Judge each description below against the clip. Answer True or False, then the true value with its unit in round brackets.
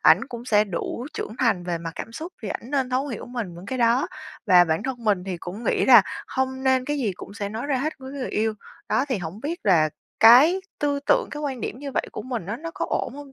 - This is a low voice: False (240 Hz)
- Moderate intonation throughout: True (4.9 semitones)